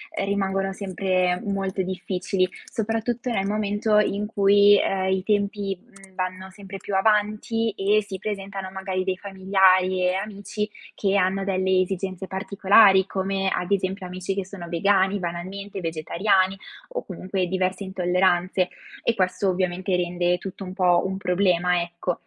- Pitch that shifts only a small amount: Yes, narrow, 1.5 semitones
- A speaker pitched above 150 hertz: Yes, high, 190 Hz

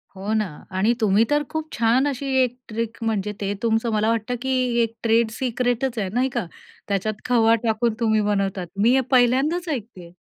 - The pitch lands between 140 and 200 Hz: No, high, 230 Hz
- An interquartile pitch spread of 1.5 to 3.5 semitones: Yes, average, 2.7 semitones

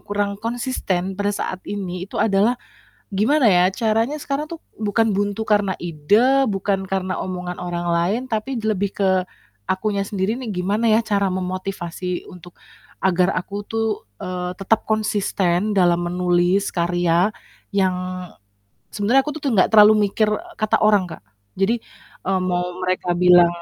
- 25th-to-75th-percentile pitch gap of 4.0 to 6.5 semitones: No, average, 3.0 semitones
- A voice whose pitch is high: Yes, high, 195 Hz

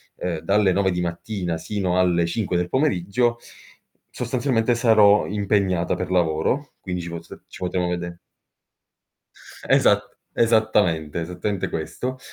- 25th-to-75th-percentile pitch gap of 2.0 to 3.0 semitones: No, average, 3.9 semitones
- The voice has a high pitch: No, very low, 95 Hz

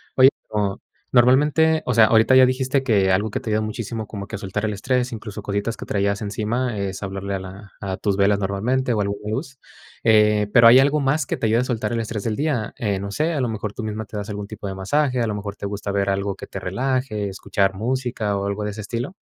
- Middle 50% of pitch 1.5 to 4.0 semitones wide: Yes, average, 3.7 semitones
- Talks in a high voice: No, low, 110 Hz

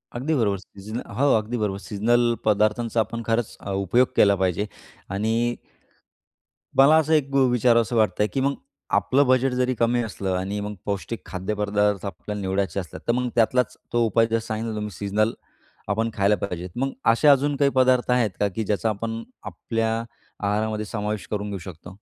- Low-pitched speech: Yes, low, 110 Hz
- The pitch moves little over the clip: No, average, 3.1 semitones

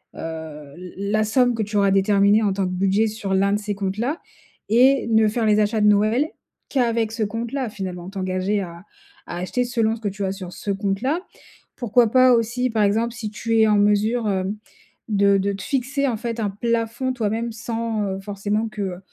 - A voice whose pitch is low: No, high, 210 Hz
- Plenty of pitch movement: No, average, 2.8 semitones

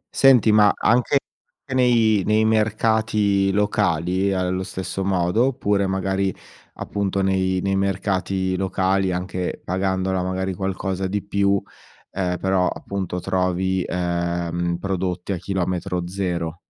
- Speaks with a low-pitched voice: Yes, very low, 95 Hz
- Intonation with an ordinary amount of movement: No, narrow, 1.7 semitones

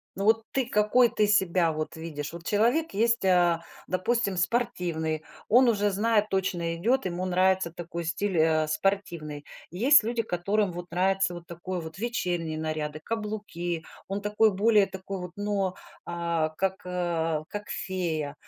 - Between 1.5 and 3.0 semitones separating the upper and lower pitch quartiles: No, average, 3.7 semitones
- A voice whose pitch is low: No, medium, 185 Hz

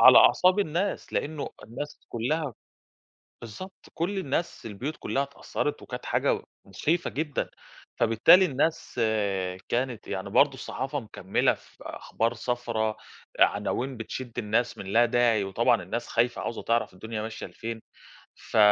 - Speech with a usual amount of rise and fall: Yes, average, 4.6 semitones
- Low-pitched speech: Yes, low, 120 Hz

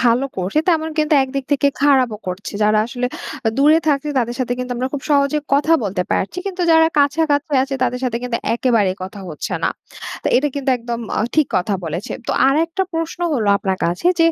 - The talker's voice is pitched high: Yes, very high, 260 Hz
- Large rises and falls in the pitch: No, average, 4.7 semitones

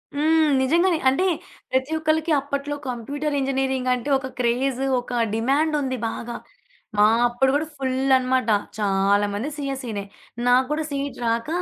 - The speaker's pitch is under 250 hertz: No, very high, 265 Hz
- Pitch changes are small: No, average, 3.3 semitones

